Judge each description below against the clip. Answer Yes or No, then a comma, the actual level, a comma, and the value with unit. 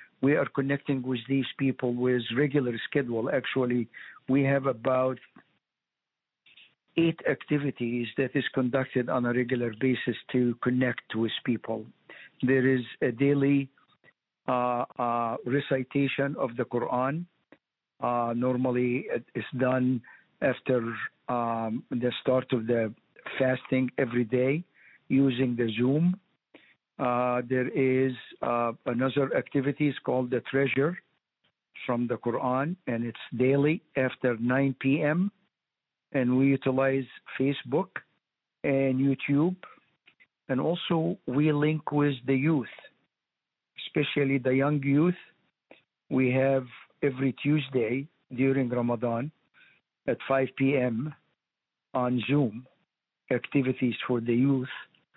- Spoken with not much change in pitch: Yes, narrow, 2.1 semitones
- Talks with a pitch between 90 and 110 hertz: No, low, 130 Hz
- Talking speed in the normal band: No, slow, 115 wpm